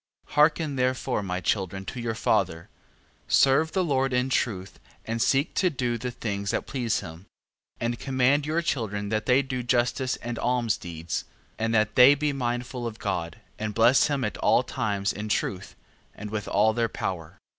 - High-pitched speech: No, low, 120 Hz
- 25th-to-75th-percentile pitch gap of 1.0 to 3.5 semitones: No, average, 4.2 semitones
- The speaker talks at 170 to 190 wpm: Yes, average, 180 wpm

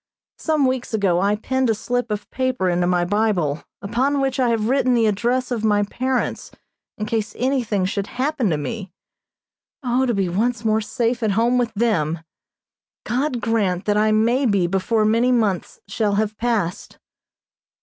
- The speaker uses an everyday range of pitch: Yes, average, 3.5 semitones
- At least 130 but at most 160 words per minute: No, average, 170 wpm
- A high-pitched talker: Yes, high, 220 Hz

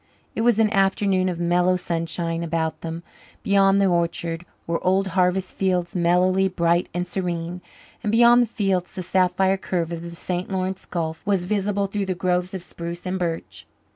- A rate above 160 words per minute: Yes, average, 175 wpm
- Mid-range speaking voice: Yes, medium, 180 Hz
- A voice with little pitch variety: Yes, narrow, 2.1 semitones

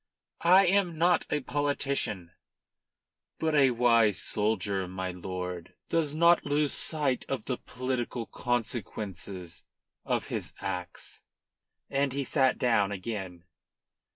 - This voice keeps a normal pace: No, slow, 115 wpm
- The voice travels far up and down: Yes, wide, 7.0 semitones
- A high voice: No, low, 120 Hz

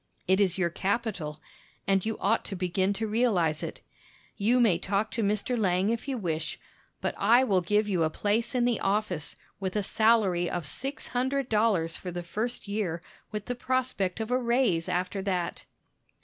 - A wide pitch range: No, average, 4.3 semitones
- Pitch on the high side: Yes, high, 205 Hz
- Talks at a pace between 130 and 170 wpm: No, average, 185 wpm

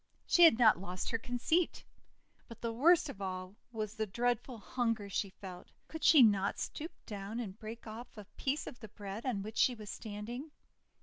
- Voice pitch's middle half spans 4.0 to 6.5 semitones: No, average, 3.4 semitones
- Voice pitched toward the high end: Yes, high, 225 Hz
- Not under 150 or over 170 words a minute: No, average, 195 wpm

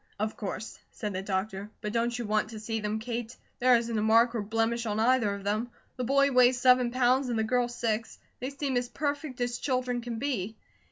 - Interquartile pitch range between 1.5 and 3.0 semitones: Yes, narrow, 2.5 semitones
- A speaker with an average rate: No, fast, 220 wpm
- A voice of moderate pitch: No, high, 235 Hz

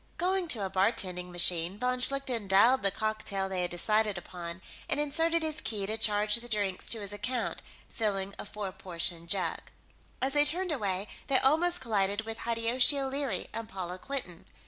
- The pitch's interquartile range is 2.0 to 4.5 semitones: No, wide, 5.4 semitones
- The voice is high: Yes, high, 215 Hz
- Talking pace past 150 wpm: Yes, average, 175 wpm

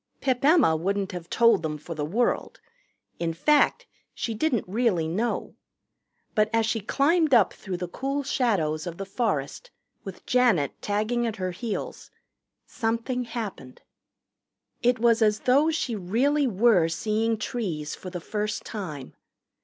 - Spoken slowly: No, average, 145 wpm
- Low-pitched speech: No, high, 215 Hz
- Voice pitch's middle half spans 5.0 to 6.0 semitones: Yes, average, 5.3 semitones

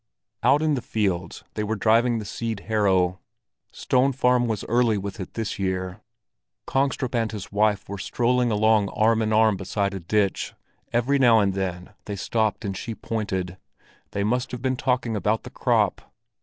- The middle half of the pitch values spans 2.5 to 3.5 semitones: Yes, average, 3.2 semitones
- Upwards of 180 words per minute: No, average, 175 wpm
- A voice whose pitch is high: No, low, 110 Hz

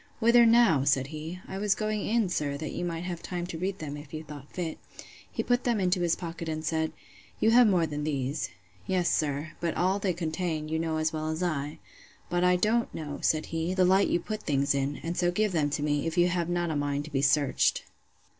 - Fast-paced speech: Yes, fast, 230 wpm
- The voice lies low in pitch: No, medium, 165 Hz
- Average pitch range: Yes, average, 3.3 semitones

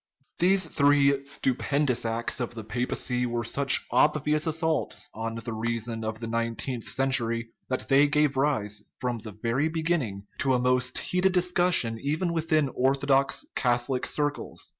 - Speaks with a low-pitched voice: Yes, low, 130 Hz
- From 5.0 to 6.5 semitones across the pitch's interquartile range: No, average, 4.3 semitones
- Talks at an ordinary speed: Yes, average, 155 wpm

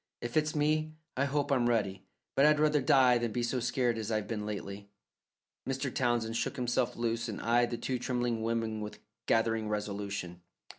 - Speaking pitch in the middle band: No, low, 120 Hz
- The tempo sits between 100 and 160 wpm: No, average, 185 wpm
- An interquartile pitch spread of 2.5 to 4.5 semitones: Yes, average, 3.2 semitones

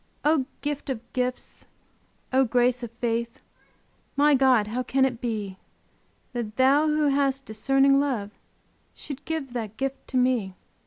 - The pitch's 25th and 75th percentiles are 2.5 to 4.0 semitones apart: Yes, average, 2.8 semitones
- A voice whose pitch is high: Yes, very high, 255 Hz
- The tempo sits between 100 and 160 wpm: Yes, average, 145 wpm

